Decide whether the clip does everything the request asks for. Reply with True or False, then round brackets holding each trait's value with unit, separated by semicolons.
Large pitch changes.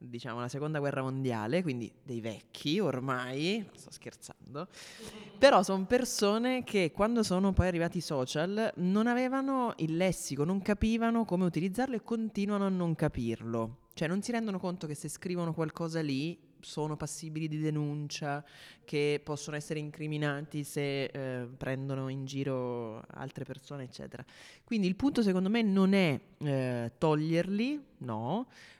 True (6.2 semitones)